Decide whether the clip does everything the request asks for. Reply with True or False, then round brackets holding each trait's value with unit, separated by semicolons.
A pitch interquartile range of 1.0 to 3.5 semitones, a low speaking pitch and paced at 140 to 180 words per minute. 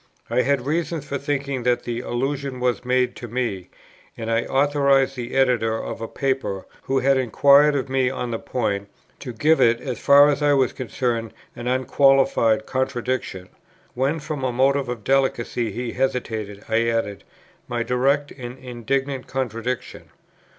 True (2.6 semitones; 130 Hz; 160 wpm)